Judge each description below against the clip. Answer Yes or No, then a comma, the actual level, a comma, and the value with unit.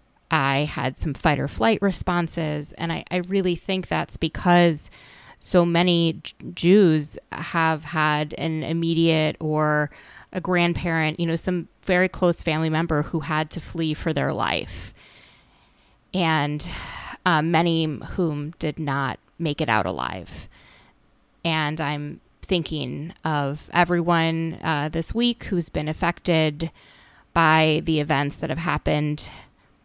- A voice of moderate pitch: Yes, medium, 160 Hz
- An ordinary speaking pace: No, slow, 130 wpm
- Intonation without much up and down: Yes, narrow, 2.2 semitones